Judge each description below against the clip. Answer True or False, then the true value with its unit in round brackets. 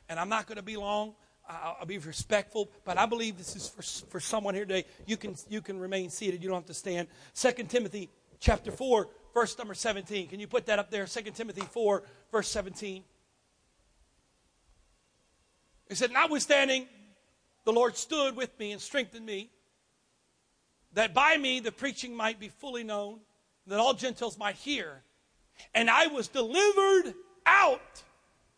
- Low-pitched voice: False (215 Hz)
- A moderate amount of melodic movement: True (3.6 semitones)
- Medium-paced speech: True (165 wpm)